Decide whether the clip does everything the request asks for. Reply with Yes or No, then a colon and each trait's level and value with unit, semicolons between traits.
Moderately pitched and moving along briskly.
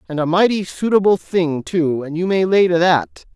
Yes: medium, 175 Hz; fast, 215 wpm